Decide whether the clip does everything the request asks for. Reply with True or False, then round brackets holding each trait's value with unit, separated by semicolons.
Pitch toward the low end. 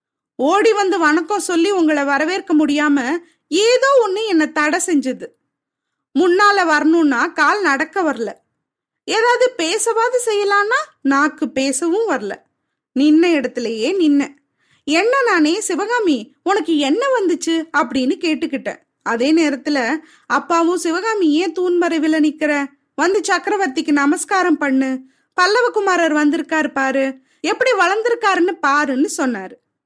False (320 Hz)